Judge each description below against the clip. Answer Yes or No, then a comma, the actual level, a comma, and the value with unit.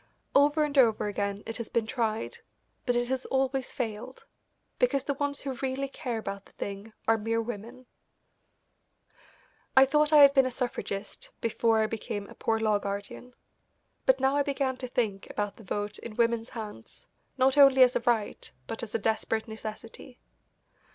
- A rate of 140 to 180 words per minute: Yes, average, 175 wpm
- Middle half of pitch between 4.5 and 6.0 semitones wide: No, average, 3.6 semitones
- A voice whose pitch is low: No, high, 235 Hz